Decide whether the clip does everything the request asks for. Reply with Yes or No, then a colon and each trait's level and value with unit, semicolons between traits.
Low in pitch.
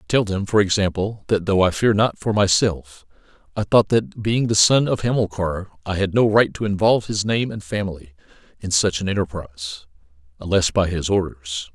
Yes: very low, 95 Hz